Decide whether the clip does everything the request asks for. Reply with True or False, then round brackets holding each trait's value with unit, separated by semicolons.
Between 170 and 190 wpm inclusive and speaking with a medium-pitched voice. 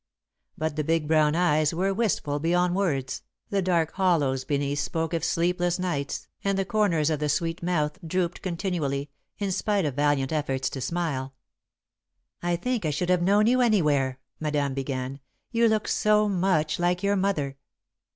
True (180 wpm; 165 Hz)